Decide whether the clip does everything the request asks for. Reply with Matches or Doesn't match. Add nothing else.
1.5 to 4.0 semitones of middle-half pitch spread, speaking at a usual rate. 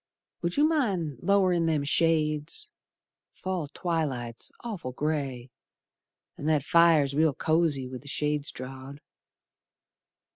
Doesn't match